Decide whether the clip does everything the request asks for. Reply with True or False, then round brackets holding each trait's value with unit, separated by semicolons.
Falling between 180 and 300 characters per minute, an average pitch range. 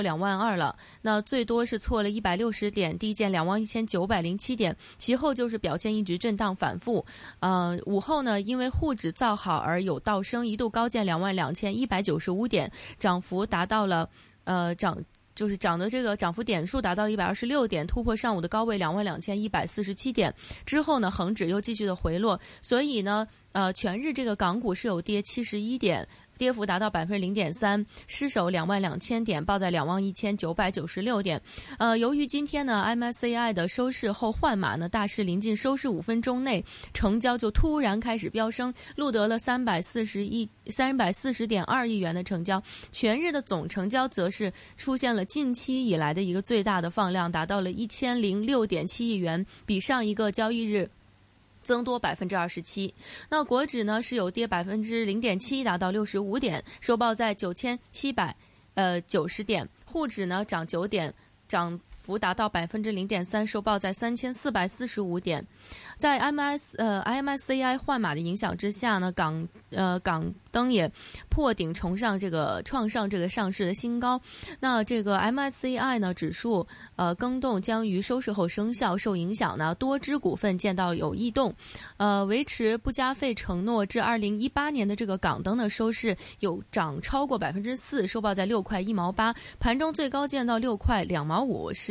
True (290 characters per minute; 4.4 semitones)